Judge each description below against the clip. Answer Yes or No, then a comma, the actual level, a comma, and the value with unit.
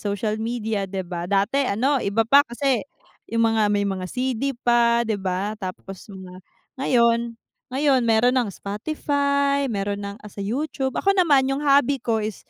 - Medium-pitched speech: No, high, 230 Hz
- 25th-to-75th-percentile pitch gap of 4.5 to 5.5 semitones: Yes, average, 4.9 semitones